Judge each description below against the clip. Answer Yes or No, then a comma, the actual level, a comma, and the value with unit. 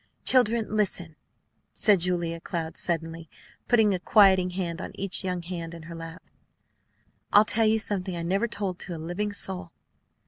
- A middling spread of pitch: Yes, average, 3.5 semitones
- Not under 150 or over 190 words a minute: Yes, average, 165 wpm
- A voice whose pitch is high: No, medium, 180 Hz